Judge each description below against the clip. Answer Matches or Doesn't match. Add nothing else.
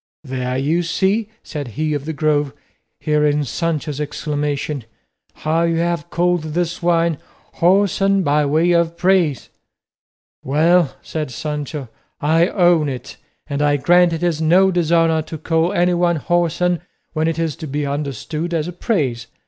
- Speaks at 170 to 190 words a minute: Doesn't match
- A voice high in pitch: Doesn't match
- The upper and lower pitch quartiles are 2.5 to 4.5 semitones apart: Matches